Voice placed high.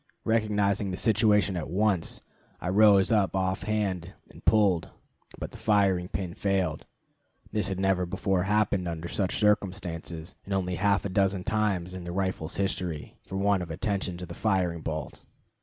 No: very low, 95 Hz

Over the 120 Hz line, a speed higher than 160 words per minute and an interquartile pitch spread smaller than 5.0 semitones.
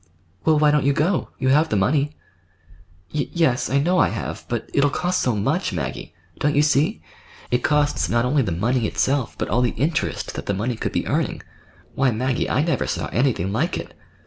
Yes: low, 135 Hz; fast, 205 wpm; average, 3.9 semitones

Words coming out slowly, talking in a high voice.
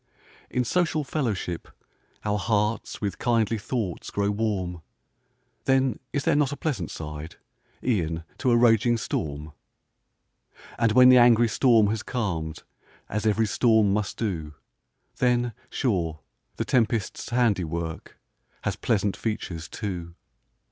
No: slow, 125 wpm; low, 110 Hz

